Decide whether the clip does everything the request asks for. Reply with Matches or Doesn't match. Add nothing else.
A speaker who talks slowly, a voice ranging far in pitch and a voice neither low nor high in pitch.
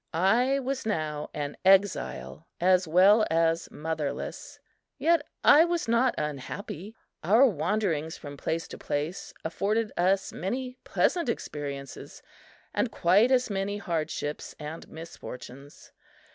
Matches